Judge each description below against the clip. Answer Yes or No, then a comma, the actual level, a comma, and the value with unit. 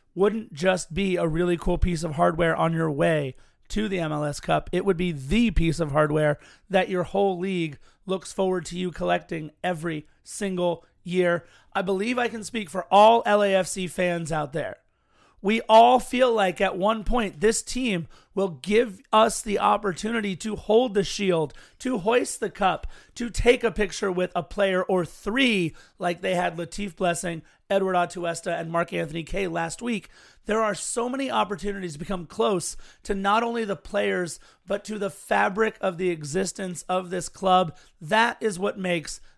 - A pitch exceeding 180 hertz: Yes, high, 190 Hz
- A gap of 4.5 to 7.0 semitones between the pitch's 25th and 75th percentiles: No, average, 3.5 semitones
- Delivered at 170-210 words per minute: Yes, average, 180 wpm